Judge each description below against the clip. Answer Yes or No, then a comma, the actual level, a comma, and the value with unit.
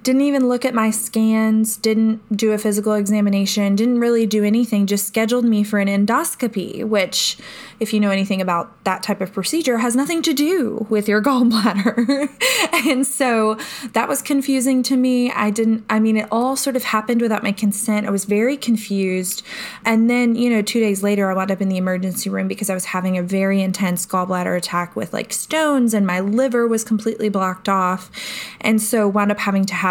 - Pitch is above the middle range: Yes, high, 215 Hz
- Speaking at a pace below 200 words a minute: No, fast, 205 wpm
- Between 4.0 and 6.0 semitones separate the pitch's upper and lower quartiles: No, average, 3.4 semitones